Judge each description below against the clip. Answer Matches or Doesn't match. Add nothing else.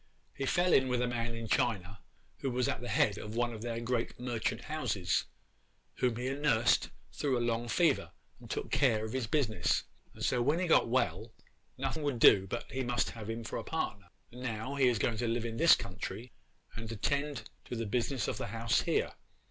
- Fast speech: Matches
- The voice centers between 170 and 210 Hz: Doesn't match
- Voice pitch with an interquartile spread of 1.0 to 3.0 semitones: Matches